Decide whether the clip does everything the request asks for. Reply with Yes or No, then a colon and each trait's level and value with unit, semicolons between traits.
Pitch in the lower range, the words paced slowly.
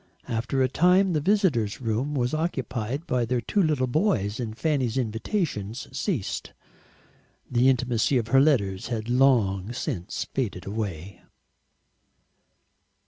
Yes: low, 125 Hz; slow, 125 wpm